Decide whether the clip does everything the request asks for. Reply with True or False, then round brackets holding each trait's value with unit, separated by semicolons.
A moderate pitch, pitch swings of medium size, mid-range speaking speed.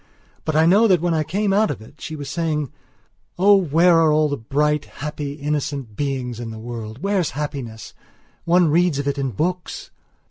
True (150 Hz; 3.9 semitones; 190 wpm)